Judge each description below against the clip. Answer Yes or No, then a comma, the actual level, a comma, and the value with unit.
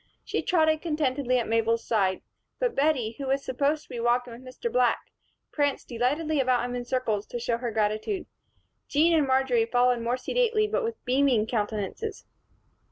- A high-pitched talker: Yes, very high, 255 Hz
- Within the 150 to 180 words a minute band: Yes, average, 170 wpm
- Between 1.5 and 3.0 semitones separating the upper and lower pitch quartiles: No, average, 4.7 semitones